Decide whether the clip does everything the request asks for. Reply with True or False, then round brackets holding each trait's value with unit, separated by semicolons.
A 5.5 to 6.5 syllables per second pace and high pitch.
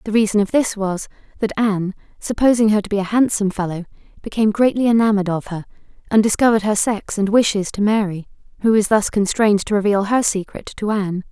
True (6.4 syllables/s; 210 Hz)